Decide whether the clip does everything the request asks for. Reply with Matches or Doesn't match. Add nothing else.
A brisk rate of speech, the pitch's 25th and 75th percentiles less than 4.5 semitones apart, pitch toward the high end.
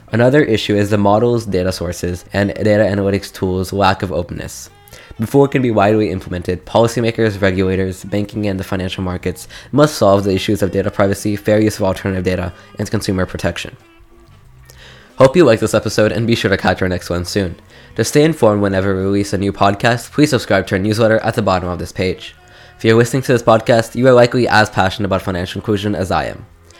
Doesn't match